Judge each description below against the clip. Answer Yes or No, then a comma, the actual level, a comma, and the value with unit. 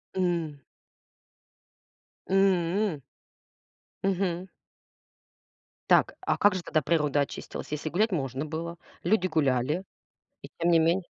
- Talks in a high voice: No, medium, 170 Hz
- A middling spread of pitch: Yes, average, 3.6 semitones